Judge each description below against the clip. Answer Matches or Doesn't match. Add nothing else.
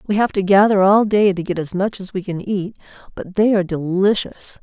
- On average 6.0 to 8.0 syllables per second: Doesn't match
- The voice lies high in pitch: Matches